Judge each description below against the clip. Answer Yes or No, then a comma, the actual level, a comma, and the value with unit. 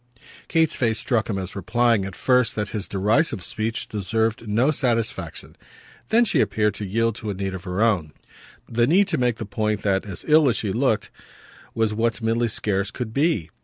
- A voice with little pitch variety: No, average, 3.2 semitones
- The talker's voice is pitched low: Yes, low, 110 Hz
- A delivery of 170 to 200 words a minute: Yes, average, 195 wpm